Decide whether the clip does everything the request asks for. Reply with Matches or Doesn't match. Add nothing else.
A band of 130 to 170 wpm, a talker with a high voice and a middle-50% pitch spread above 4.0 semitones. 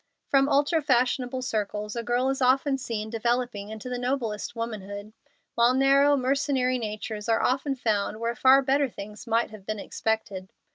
Doesn't match